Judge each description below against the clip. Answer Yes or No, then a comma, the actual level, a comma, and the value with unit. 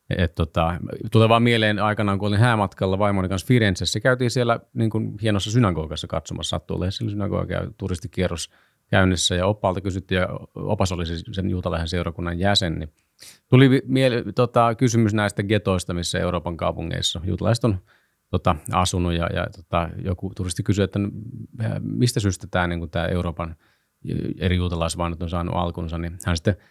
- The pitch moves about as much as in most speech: Yes, average, 4.2 semitones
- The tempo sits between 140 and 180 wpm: Yes, average, 150 wpm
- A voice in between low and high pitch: No, very low, 95 Hz